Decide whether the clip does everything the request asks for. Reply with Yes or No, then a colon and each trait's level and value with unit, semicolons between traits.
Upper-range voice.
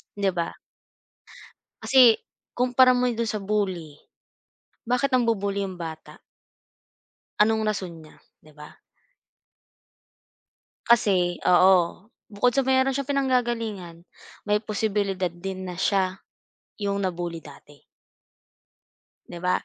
Yes: high, 200 Hz